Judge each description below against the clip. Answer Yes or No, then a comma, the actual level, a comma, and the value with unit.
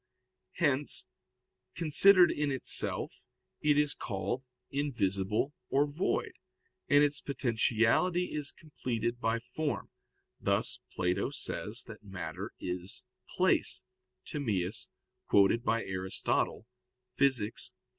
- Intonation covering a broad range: Yes, wide, 6.4 semitones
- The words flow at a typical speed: No, slow, 95 wpm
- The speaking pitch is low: Yes, low, 120 Hz